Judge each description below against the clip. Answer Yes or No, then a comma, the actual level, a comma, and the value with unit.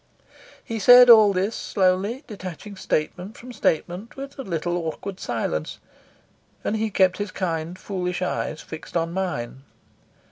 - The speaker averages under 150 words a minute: Yes, average, 140 wpm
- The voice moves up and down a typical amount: Yes, average, 3.8 semitones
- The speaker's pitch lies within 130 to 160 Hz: No, medium, 185 Hz